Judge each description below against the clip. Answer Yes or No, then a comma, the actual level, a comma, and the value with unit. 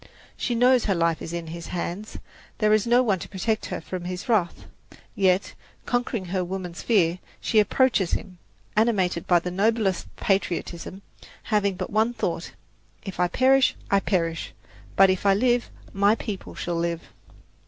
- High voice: Yes, high, 195 Hz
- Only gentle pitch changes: No, average, 3.8 semitones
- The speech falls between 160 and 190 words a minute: Yes, average, 165 wpm